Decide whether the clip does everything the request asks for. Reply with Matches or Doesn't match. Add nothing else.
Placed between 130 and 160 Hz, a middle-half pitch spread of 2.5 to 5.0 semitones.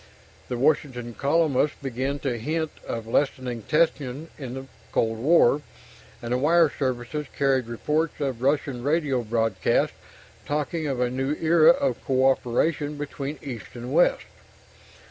Matches